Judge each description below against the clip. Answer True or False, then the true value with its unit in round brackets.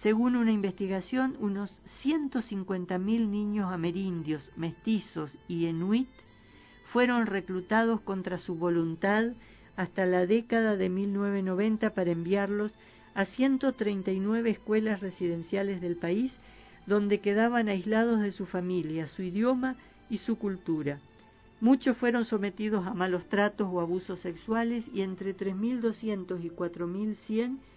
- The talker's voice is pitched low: False (200 Hz)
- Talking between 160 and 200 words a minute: False (130 wpm)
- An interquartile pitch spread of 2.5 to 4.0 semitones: True (3.5 semitones)